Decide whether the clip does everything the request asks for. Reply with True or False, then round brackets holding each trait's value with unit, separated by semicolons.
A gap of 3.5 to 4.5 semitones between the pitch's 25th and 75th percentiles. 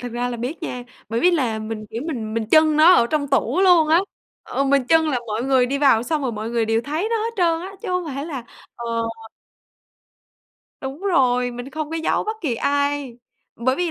False (5.1 semitones)